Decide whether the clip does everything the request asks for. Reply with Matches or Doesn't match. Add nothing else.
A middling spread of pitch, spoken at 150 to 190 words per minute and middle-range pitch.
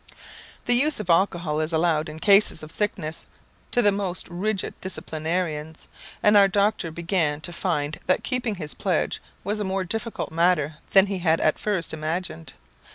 Matches